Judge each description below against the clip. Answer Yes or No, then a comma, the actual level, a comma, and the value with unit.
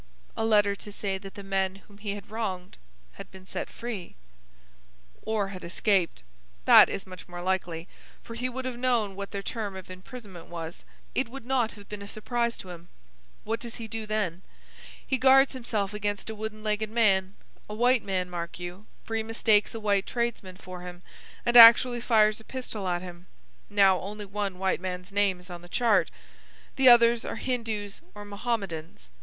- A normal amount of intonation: Yes, average, 3.4 semitones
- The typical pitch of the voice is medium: No, high, 205 Hz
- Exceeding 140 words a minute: Yes, average, 185 wpm